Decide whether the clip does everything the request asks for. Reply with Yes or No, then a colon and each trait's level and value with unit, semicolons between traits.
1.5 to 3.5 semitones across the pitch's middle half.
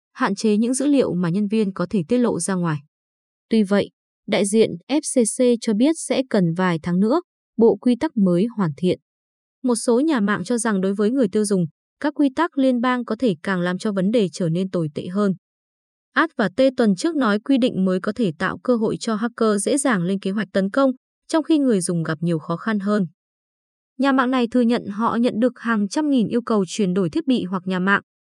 No: average, 4.7 semitones